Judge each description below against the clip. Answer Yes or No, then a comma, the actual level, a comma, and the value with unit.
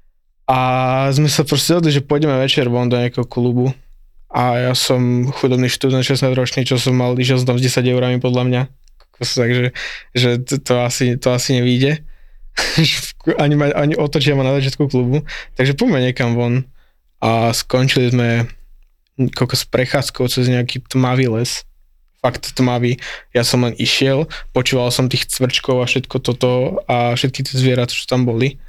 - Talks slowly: No, fast, 165 wpm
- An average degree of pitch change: No, narrow, 1.6 semitones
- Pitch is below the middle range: Yes, low, 125 Hz